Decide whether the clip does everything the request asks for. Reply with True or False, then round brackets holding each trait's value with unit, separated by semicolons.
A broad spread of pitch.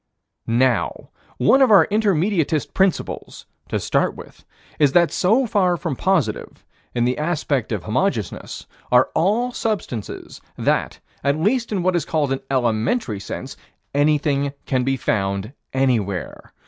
True (7.3 semitones)